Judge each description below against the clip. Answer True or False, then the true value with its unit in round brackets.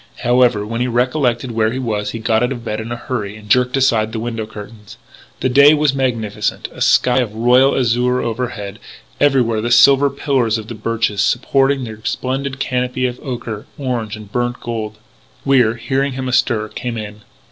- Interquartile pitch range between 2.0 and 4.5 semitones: True (2.7 semitones)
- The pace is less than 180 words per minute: False (190 wpm)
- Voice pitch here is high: False (120 Hz)